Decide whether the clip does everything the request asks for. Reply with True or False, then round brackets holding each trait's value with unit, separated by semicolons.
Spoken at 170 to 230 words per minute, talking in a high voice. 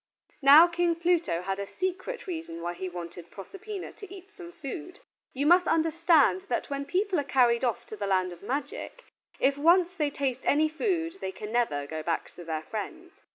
True (195 wpm; 285 Hz)